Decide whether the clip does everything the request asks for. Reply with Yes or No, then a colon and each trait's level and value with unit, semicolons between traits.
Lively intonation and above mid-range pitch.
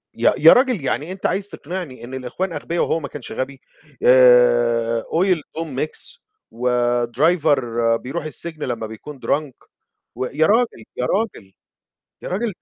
No: wide, 5.9 semitones; medium, 140 Hz